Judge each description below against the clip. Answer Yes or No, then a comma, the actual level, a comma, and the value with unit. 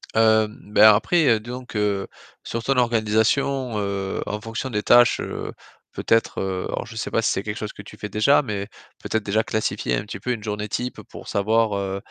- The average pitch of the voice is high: No, low, 110 Hz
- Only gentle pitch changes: Yes, narrow, 2.0 semitones